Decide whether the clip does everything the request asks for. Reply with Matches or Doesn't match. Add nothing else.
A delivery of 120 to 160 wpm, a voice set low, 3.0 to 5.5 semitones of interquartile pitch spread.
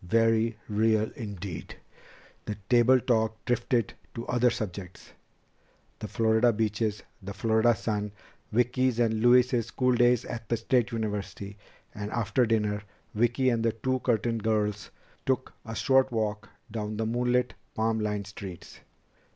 Doesn't match